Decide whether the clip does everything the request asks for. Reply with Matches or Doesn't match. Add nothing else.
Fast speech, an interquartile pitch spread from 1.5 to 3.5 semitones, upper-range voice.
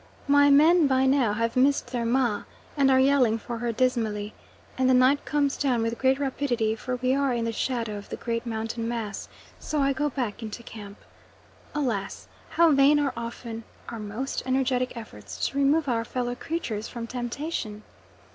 Doesn't match